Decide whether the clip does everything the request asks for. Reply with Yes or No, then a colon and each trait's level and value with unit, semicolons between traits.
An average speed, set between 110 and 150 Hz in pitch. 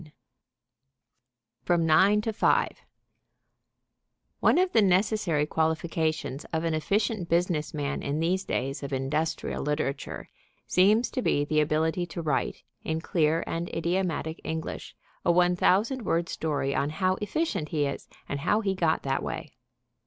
No: average, 145 wpm; medium, 165 Hz